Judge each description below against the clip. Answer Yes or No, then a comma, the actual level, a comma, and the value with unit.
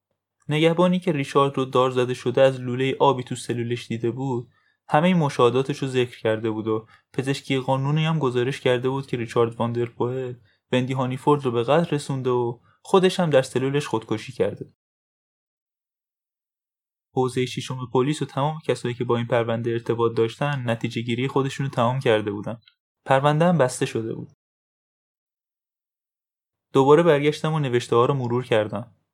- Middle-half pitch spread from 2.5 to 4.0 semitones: Yes, average, 2.8 semitones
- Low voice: Yes, low, 130 Hz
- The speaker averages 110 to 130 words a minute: No, fast, 155 wpm